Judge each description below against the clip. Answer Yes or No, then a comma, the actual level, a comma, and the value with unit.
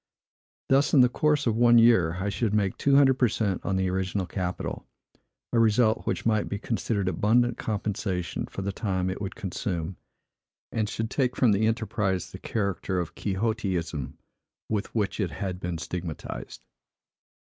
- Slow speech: No, average, 165 wpm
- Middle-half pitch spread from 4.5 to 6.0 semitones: No, average, 3.6 semitones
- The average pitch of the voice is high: No, low, 105 Hz